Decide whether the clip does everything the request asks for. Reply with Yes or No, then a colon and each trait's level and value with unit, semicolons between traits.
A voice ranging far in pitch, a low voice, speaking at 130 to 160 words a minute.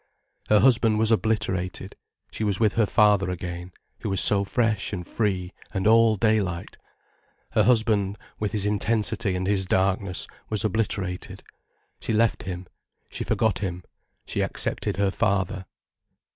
No: average, 2.7 semitones; low, 100 Hz; average, 145 wpm